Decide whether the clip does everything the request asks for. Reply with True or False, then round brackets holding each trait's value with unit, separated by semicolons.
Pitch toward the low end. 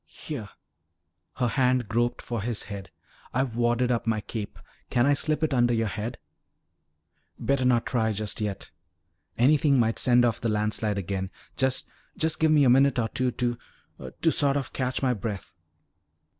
True (120 Hz)